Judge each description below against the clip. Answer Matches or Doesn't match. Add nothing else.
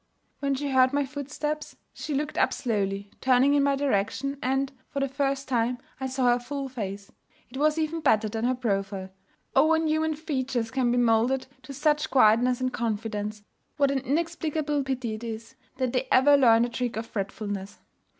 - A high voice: Matches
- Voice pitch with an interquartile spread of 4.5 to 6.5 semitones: Doesn't match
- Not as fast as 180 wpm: Doesn't match